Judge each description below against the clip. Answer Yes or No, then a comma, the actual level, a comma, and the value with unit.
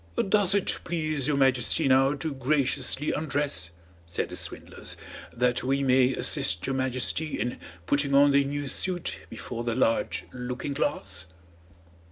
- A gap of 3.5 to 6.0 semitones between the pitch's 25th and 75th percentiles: No, narrow, 2.6 semitones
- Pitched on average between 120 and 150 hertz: Yes, low, 135 Hz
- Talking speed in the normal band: Yes, average, 145 wpm